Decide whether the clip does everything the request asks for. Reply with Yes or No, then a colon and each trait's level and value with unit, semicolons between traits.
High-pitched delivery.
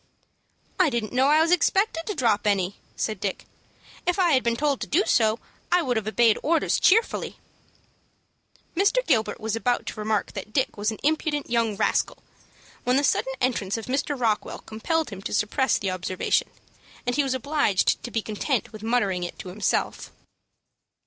Yes: high, 240 Hz